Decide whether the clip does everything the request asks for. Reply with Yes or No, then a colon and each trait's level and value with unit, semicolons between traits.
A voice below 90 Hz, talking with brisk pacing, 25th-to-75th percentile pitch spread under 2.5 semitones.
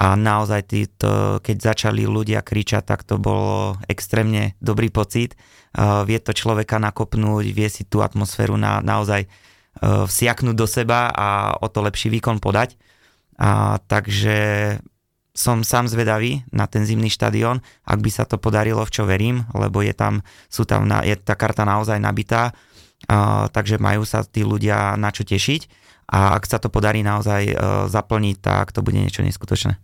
No: low, 110 Hz; fast, 170 wpm; narrow, 1.8 semitones